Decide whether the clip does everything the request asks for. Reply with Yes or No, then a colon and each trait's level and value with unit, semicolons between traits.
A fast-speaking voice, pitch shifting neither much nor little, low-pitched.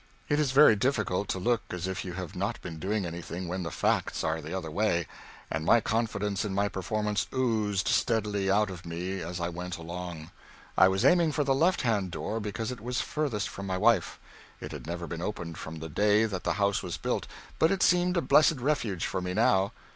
Yes: fast, 220 wpm; average, 4.2 semitones; low, 100 Hz